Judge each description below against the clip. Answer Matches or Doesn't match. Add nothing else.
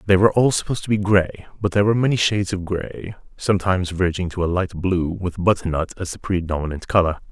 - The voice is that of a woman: Doesn't match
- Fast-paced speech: Matches